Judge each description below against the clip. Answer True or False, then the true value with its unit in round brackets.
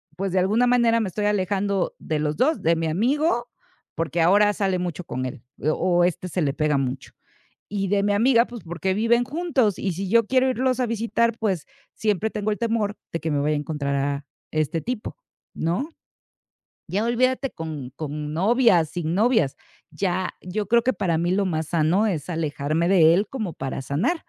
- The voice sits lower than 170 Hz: False (190 Hz)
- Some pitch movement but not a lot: False (6.1 semitones)